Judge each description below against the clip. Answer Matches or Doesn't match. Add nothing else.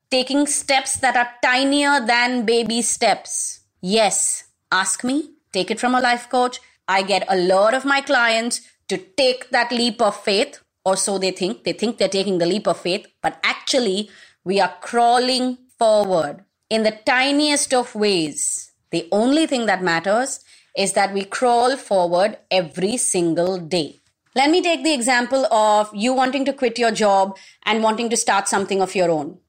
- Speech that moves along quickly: Doesn't match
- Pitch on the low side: Doesn't match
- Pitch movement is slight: Doesn't match